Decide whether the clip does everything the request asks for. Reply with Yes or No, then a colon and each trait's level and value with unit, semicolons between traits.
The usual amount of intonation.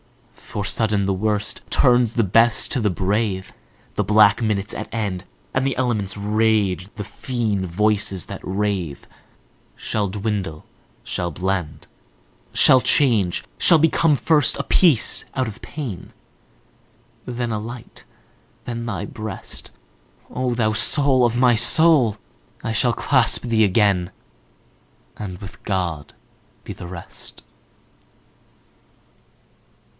Yes: average, 3.7 semitones